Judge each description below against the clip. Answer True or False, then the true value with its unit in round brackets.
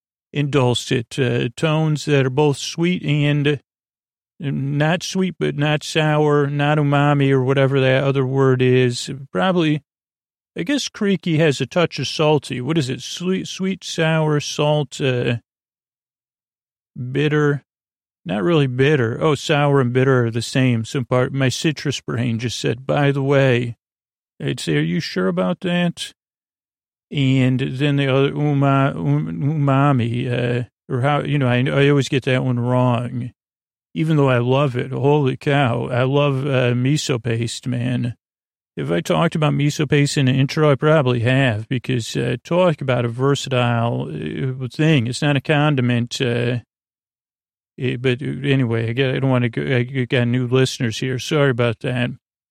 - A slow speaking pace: False (160 wpm)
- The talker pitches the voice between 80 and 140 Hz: True (135 Hz)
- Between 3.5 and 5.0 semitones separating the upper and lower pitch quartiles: False (3.0 semitones)